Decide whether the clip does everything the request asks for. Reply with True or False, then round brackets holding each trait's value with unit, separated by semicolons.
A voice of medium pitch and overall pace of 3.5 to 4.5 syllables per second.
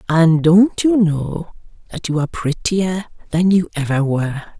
True (170 Hz; 4.4 syllables/s)